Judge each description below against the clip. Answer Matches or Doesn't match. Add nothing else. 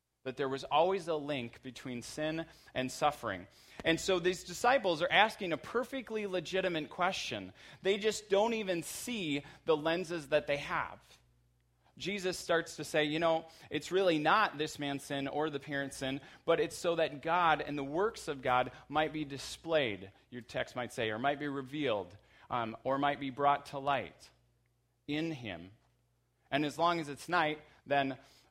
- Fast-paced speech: Doesn't match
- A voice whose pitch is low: Doesn't match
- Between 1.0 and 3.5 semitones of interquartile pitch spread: Doesn't match